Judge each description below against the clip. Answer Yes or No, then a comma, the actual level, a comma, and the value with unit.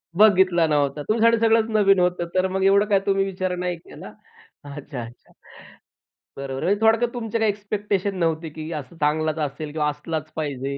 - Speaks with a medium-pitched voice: Yes, medium, 180 Hz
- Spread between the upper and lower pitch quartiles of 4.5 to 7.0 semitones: Yes, average, 5.1 semitones